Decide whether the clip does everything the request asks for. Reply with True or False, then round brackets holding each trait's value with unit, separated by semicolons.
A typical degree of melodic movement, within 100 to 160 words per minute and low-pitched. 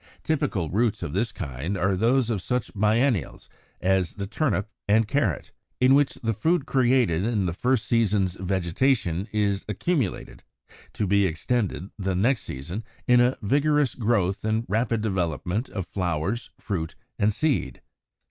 True (4.6 semitones; 150 wpm; 105 Hz)